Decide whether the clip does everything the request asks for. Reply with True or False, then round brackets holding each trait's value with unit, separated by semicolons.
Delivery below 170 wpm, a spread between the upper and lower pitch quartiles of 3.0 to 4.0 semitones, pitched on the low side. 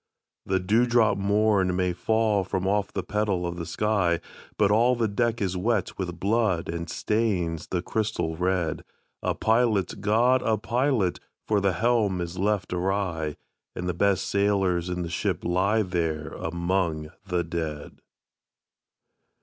True (150 wpm; 3.6 semitones; 95 Hz)